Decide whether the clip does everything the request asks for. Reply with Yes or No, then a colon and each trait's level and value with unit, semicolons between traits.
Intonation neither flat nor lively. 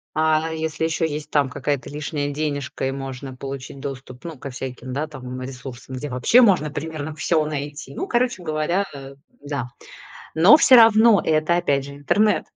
Yes: average, 3.1 semitones